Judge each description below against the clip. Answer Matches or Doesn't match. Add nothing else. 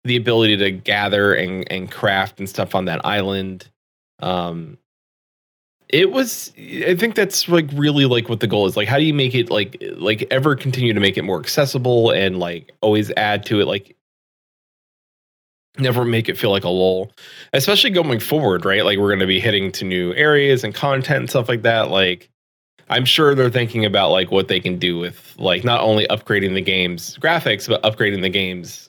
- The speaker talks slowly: Doesn't match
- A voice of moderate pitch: Doesn't match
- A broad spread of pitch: Matches